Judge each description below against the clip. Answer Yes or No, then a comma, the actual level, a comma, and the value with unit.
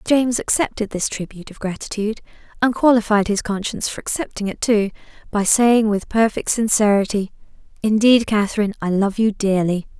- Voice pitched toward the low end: No, high, 210 Hz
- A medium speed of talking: Yes, average, 150 wpm